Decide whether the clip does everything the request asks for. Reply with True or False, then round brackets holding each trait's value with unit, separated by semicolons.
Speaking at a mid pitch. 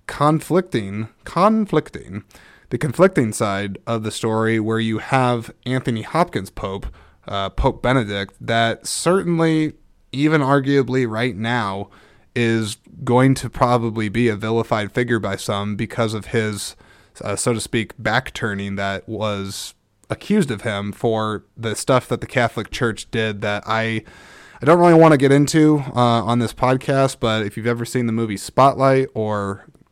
False (115 Hz)